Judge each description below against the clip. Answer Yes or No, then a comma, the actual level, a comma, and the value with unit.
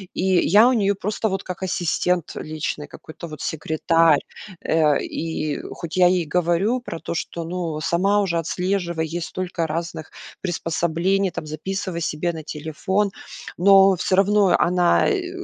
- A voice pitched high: No, medium, 175 Hz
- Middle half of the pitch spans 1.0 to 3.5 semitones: Yes, average, 3.1 semitones